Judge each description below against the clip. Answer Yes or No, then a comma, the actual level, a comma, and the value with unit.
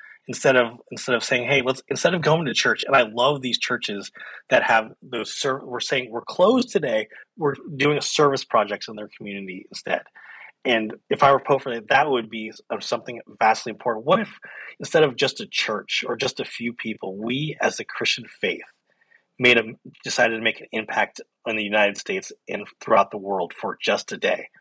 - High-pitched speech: No, low, 125 Hz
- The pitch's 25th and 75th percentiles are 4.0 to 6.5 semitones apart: Yes, average, 4.5 semitones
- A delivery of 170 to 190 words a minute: No, fast, 205 wpm